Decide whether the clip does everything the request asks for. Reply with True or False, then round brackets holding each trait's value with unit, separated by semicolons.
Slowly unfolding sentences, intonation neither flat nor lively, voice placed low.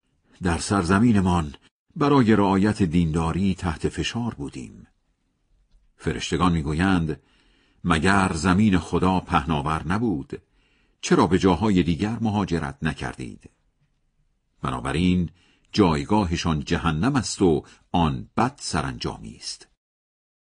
True (90 wpm; 3.4 semitones; 90 Hz)